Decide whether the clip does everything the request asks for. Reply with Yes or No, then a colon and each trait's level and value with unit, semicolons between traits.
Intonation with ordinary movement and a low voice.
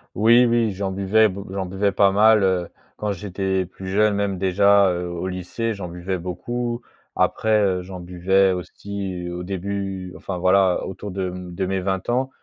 No: narrow, 1.8 semitones; very low, 95 Hz